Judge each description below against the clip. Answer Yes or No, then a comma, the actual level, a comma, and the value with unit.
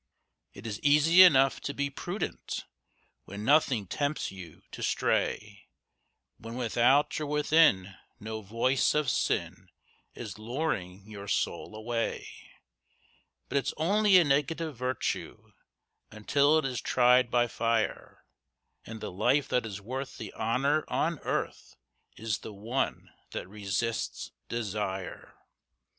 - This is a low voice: Yes, low, 120 Hz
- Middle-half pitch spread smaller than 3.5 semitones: No, average, 5.0 semitones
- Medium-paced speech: No, slow, 125 wpm